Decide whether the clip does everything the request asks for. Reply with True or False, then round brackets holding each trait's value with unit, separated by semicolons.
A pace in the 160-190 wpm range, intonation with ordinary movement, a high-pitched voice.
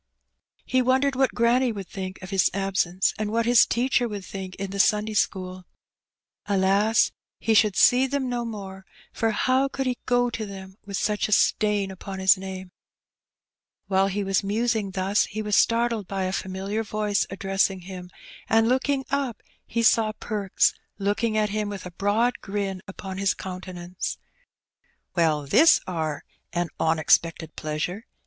True (165 wpm; 3.1 semitones; 200 Hz)